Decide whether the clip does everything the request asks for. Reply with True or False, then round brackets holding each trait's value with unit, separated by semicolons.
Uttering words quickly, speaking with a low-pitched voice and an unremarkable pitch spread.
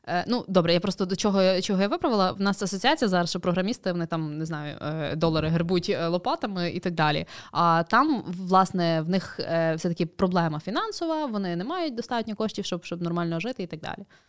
False (195 wpm; 185 Hz; 3.1 semitones)